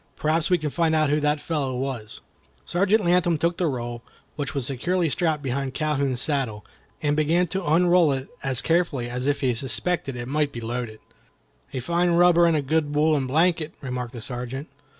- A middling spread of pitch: Yes, average, 4.5 semitones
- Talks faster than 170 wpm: Yes, average, 190 wpm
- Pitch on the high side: No, medium, 150 Hz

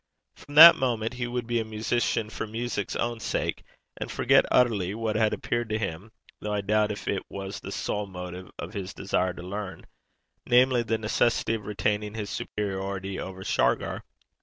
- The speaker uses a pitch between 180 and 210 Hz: No, low, 105 Hz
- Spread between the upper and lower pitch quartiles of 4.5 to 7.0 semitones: No, average, 2.8 semitones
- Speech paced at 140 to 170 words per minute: No, average, 180 wpm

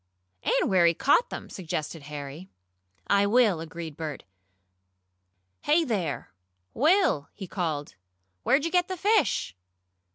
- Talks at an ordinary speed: No, slow, 125 wpm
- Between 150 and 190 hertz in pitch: Yes, medium, 185 Hz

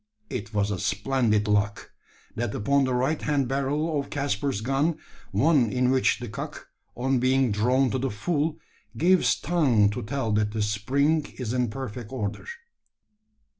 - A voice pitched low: Yes, low, 130 Hz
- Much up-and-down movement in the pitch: No, average, 4.7 semitones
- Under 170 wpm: Yes, average, 160 wpm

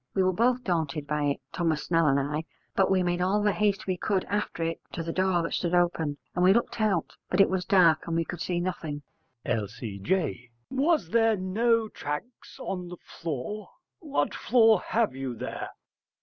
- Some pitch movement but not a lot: Yes, average, 4.5 semitones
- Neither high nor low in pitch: Yes, medium, 180 Hz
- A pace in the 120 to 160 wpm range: No, average, 200 wpm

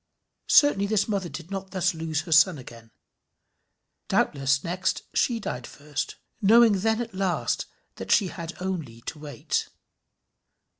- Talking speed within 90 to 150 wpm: Yes, average, 140 wpm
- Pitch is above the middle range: No, medium, 180 Hz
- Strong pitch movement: No, average, 4.9 semitones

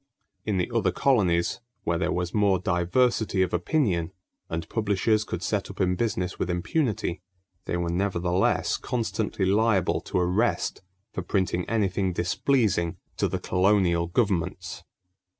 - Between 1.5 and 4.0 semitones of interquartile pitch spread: Yes, average, 3.2 semitones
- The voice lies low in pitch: Yes, very low, 95 Hz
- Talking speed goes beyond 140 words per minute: No, slow, 135 wpm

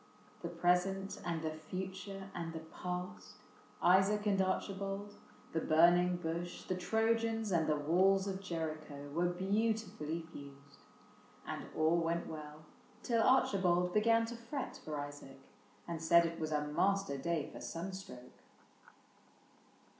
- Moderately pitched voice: Yes, medium, 175 Hz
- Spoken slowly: Yes, slow, 130 wpm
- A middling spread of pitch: Yes, average, 3.6 semitones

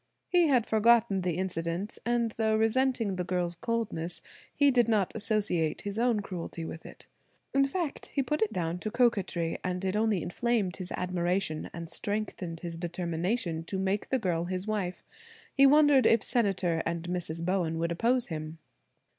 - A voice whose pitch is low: No, high, 195 Hz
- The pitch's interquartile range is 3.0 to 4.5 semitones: No, average, 5.1 semitones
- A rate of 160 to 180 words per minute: Yes, average, 170 wpm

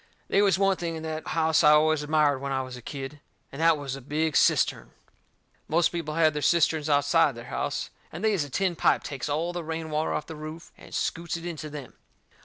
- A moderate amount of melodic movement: No, narrow, 2.3 semitones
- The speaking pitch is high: No, medium, 155 Hz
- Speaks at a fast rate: Yes, fast, 230 wpm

